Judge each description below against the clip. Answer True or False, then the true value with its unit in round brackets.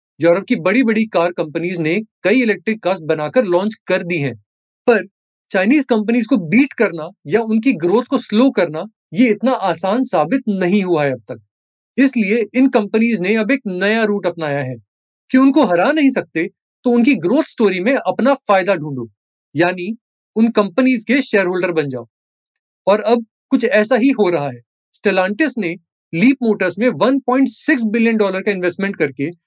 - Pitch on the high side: True (210 Hz)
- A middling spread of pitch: False (5.9 semitones)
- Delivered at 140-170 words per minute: False (110 wpm)